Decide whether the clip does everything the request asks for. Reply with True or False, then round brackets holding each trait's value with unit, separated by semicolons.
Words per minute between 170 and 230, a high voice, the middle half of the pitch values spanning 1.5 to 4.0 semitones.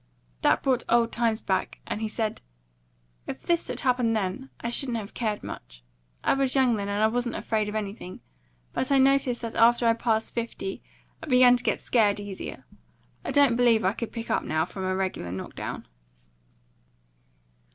True (190 wpm; 230 Hz; 3.3 semitones)